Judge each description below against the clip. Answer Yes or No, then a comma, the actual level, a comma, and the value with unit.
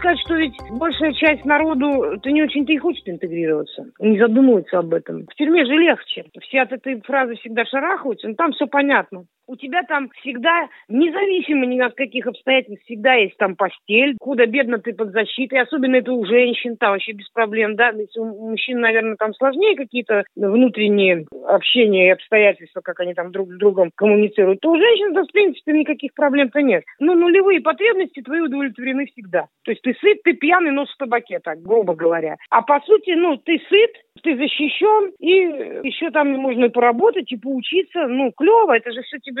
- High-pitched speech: Yes, very high, 260 Hz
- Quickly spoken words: Yes, fast, 185 wpm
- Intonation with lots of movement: Yes, wide, 5.9 semitones